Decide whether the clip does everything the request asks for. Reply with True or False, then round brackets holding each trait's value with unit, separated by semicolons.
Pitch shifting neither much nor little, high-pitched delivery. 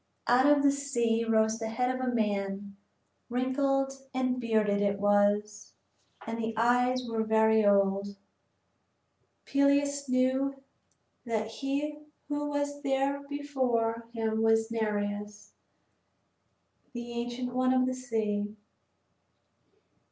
True (3.2 semitones; 235 Hz)